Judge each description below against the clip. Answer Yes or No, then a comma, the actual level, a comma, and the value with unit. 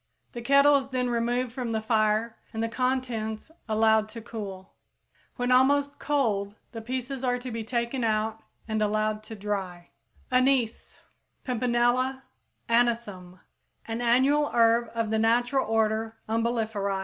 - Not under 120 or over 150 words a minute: Yes, average, 140 wpm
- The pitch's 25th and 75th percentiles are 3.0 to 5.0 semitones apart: No, narrow, 2.5 semitones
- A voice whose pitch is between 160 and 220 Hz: No, high, 230 Hz